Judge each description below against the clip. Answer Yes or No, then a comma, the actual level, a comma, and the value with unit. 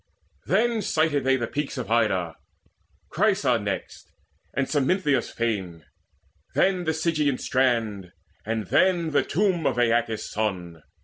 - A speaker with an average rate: No, slow, 125 wpm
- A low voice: Yes, low, 130 Hz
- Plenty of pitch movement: Yes, wide, 6.4 semitones